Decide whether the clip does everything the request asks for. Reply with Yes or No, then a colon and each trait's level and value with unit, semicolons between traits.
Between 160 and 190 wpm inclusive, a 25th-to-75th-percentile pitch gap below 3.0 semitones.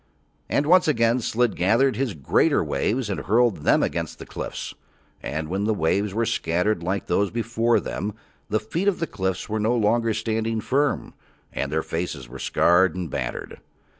No: average, 175 wpm; average, 4.3 semitones